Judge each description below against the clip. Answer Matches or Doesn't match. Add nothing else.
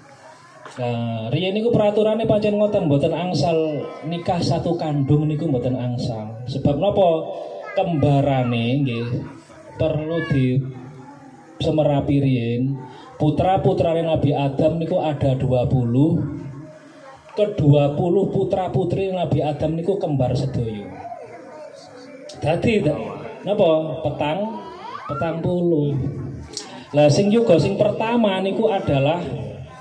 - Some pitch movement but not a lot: Matches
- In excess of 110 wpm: Doesn't match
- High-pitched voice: Doesn't match